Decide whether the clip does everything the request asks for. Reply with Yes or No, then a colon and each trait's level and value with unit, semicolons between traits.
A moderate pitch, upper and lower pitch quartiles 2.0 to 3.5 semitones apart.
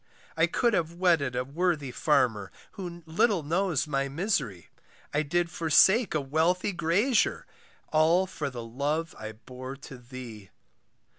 No: medium, 155 Hz; average, 5.2 semitones